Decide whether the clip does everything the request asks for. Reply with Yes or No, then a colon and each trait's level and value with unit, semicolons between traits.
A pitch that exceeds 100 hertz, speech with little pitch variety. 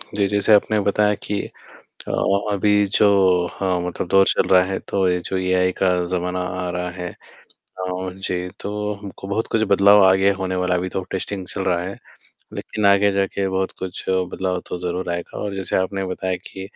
No: very low, 95 Hz; narrow, 1.5 semitones